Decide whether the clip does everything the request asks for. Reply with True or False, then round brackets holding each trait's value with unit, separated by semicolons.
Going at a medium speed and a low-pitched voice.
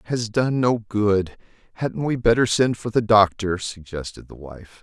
True (185 wpm; 105 Hz)